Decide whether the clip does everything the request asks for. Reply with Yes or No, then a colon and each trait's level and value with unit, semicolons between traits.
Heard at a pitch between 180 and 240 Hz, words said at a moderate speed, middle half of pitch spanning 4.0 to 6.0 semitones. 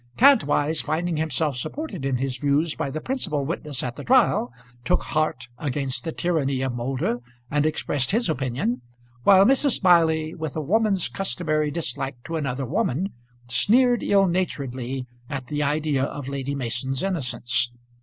No: medium, 150 Hz; average, 155 wpm; average, 4.7 semitones